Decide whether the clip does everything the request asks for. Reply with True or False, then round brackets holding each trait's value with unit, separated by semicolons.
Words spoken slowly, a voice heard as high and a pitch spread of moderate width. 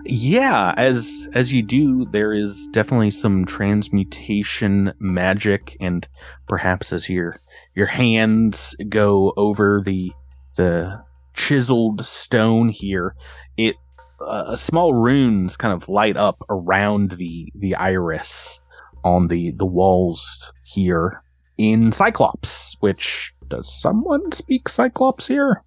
False (115 wpm; 100 Hz; 4.0 semitones)